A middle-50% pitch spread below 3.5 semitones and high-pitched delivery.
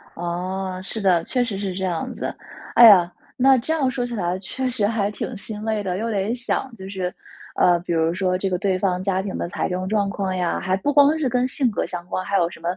No: average, 4.1 semitones; high, 195 Hz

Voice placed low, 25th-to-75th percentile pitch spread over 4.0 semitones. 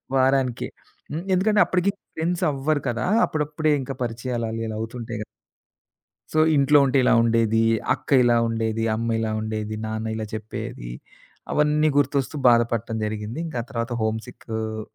Yes: low, 120 Hz; average, 4.4 semitones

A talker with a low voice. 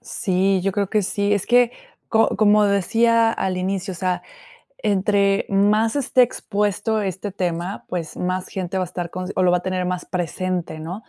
No: high, 195 Hz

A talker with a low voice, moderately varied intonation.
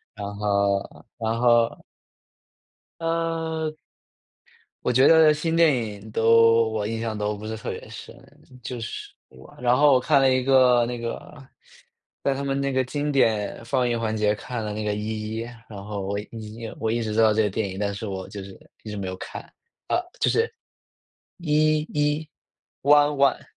Yes: low, 115 Hz; average, 4.6 semitones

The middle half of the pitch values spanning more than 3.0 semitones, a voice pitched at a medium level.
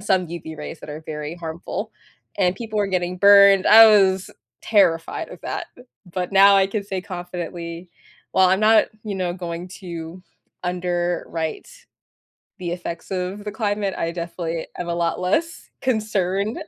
No: average, 2.7 semitones; medium, 180 Hz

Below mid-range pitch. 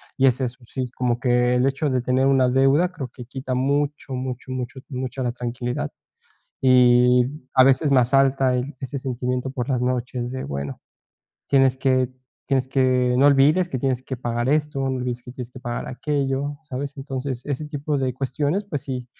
Yes: low, 130 Hz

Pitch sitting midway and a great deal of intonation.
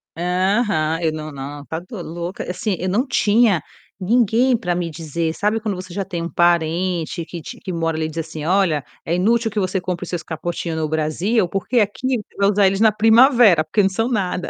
No: medium, 180 Hz; average, 4.1 semitones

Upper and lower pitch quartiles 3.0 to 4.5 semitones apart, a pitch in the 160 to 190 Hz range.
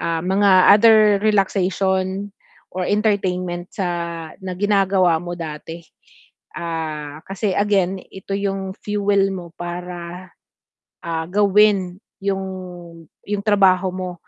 No: narrow, 2.4 semitones; medium, 185 Hz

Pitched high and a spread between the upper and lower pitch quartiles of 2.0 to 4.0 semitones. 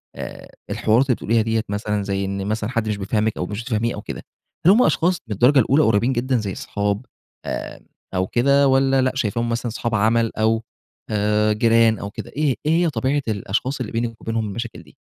No: low, 115 Hz; average, 3.4 semitones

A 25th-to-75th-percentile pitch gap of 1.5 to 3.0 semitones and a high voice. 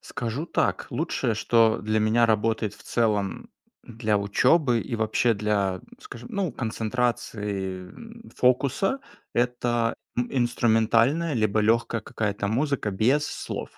No: average, 2.7 semitones; low, 115 Hz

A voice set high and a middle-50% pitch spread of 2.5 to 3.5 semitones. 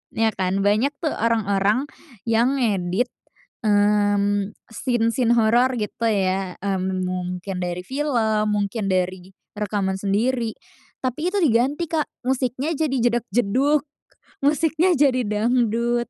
No: high, 225 Hz; average, 4.3 semitones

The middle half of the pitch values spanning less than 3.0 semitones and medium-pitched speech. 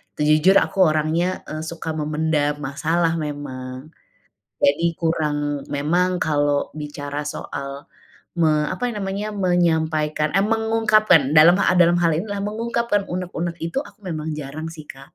No: average, 3.3 semitones; medium, 160 Hz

